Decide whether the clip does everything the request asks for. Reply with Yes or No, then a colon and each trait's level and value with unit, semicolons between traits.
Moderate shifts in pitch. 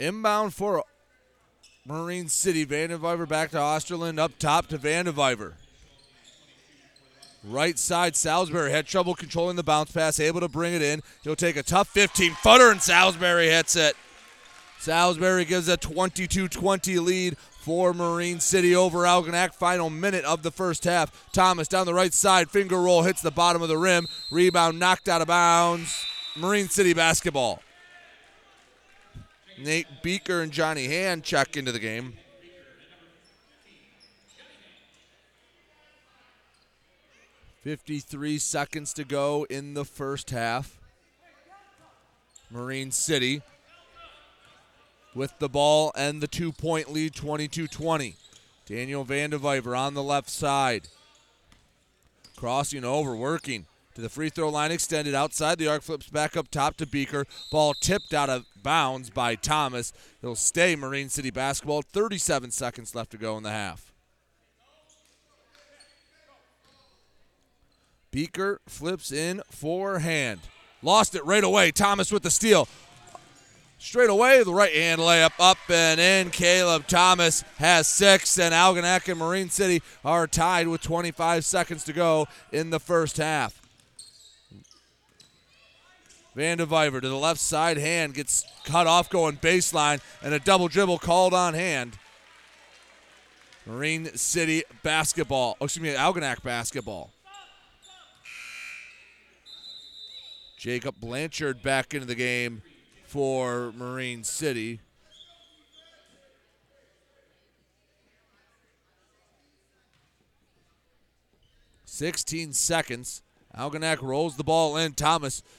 Yes: average, 4.1 semitones